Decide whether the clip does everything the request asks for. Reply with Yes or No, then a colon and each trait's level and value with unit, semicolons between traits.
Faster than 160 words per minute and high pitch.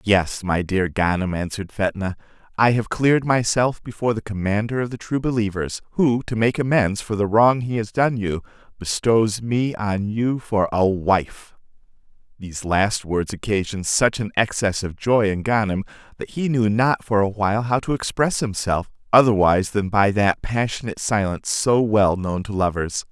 No: average, 175 wpm; low, 105 Hz